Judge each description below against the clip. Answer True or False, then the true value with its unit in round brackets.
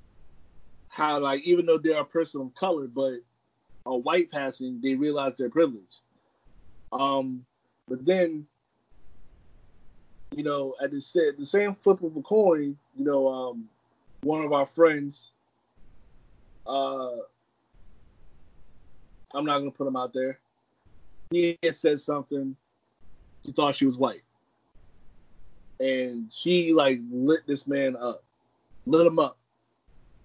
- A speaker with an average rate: False (125 wpm)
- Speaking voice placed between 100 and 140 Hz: True (135 Hz)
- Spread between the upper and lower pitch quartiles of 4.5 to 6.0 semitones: False (3.2 semitones)